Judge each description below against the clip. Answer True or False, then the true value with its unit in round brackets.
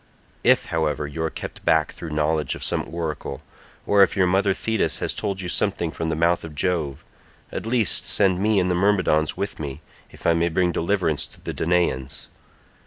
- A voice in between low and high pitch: False (85 Hz)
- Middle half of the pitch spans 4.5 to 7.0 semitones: False (3.5 semitones)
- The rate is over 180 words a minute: True (195 wpm)